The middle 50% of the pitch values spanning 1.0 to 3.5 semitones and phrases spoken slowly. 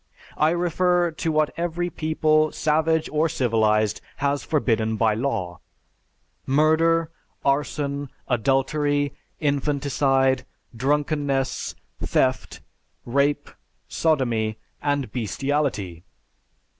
Yes: average, 3.1 semitones; slow, 80 wpm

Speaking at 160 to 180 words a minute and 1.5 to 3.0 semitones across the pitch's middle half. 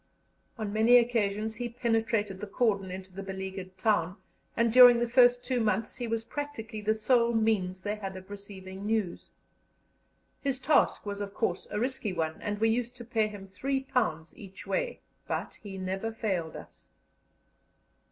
No: average, 165 wpm; average, 3.6 semitones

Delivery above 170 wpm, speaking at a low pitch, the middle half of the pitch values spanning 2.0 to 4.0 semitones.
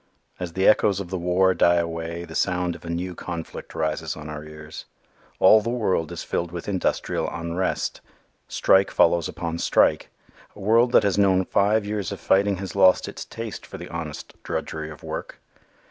Yes: average, 185 wpm; very low, 90 Hz; average, 2.8 semitones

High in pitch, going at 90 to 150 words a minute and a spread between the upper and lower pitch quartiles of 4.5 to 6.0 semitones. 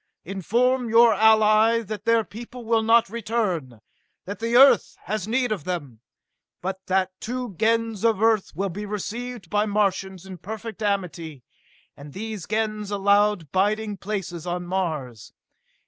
No: high, 210 Hz; average, 145 wpm; average, 3.3 semitones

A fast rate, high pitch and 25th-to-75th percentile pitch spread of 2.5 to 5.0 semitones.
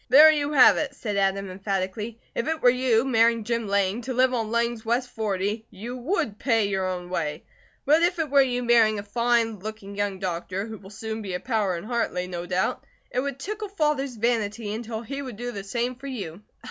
Yes: fast, 215 wpm; high, 225 Hz; average, 4.0 semitones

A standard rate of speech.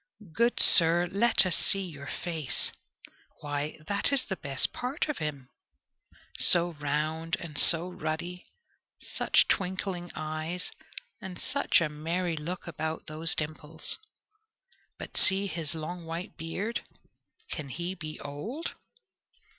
No: slow, 125 wpm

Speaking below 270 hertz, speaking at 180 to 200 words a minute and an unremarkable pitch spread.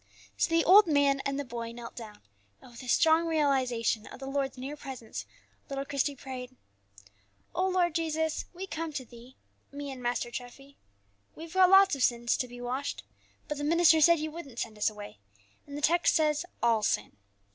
No: very high, 275 Hz; average, 190 wpm; average, 4.6 semitones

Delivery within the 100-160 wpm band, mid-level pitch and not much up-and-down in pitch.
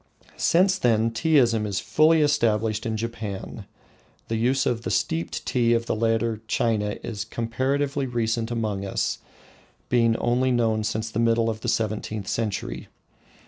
No: average, 145 wpm; low, 115 Hz; narrow, 1.9 semitones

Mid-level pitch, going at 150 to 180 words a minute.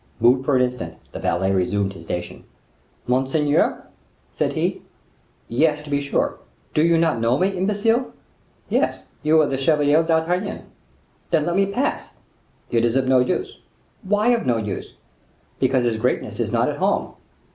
Yes: medium, 145 Hz; average, 165 wpm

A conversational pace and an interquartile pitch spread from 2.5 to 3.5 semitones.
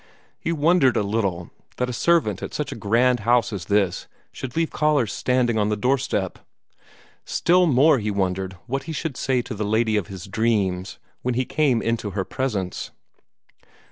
No: average, 175 wpm; average, 4.5 semitones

